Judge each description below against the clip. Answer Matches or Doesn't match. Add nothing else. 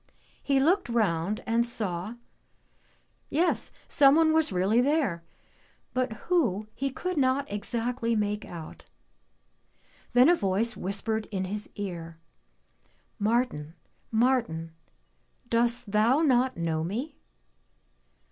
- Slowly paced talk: Matches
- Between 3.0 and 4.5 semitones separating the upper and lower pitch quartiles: Doesn't match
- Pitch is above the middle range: Matches